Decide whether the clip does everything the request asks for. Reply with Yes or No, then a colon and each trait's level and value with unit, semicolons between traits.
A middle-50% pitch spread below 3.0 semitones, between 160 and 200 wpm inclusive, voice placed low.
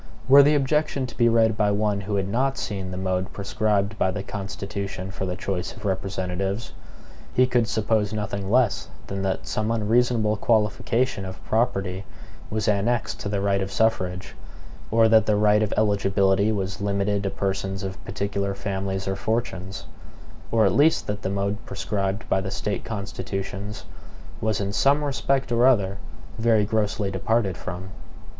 Yes: narrow, 2.4 semitones; average, 165 wpm; low, 100 Hz